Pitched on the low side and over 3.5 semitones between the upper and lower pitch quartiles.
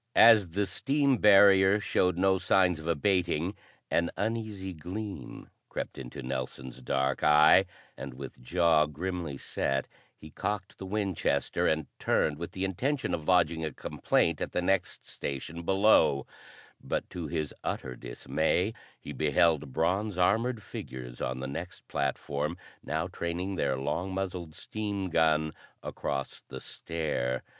Yes: very low, 85 Hz; average, 4.8 semitones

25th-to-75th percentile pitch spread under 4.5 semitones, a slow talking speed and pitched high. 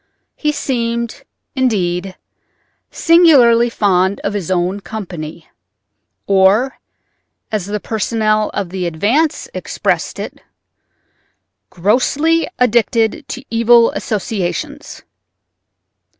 Yes: average, 4.1 semitones; slow, 80 wpm; high, 215 Hz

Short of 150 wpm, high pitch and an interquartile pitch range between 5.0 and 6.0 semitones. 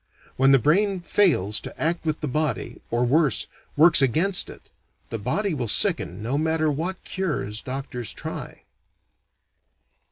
No: average, 140 wpm; medium, 150 Hz; wide, 5.4 semitones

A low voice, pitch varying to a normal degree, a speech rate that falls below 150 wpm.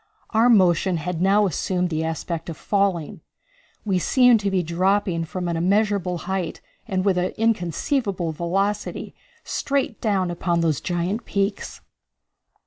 No: medium, 185 Hz; average, 3.0 semitones; slow, 135 wpm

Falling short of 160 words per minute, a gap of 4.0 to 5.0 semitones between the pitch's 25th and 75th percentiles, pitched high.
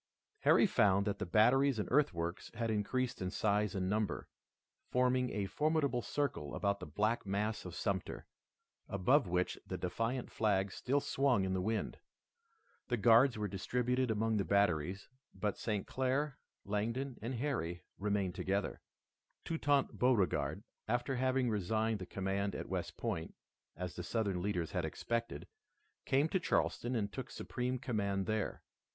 No: average, 150 wpm; average, 4.4 semitones; low, 110 Hz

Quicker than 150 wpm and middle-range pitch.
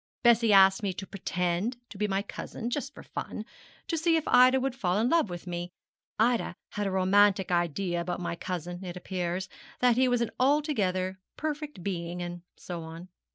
No: average, 190 wpm; high, 195 Hz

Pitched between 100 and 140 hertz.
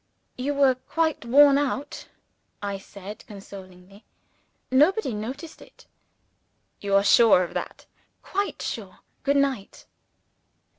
No: very high, 250 Hz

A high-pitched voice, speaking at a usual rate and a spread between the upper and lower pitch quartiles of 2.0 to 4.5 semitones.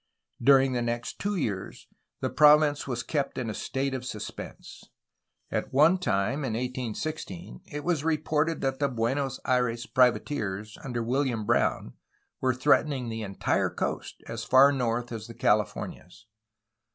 No: low, 125 Hz; average, 150 wpm; average, 3.7 semitones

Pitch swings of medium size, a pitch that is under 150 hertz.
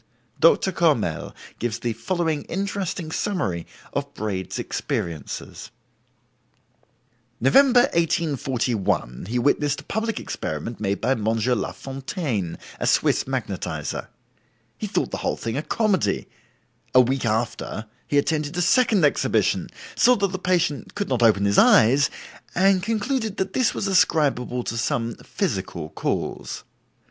No: wide, 8.7 semitones; medium, 140 Hz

